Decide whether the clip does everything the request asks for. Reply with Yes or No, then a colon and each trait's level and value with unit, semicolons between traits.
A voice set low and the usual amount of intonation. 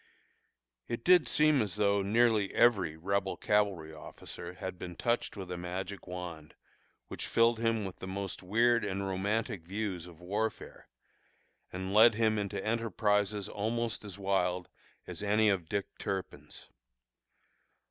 Yes: low, 100 Hz; average, 3.1 semitones